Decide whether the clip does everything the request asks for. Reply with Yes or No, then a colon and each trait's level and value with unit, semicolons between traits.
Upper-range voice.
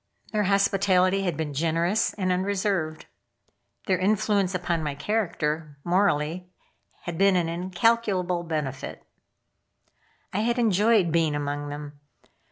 No: medium, 180 Hz